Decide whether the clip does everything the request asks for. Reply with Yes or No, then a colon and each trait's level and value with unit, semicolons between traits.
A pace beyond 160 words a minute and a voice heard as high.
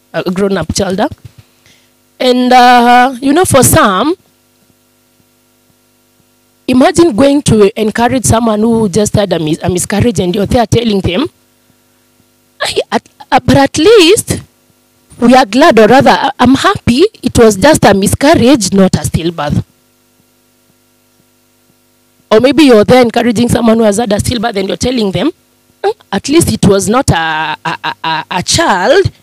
No: average, 150 wpm; high, 215 Hz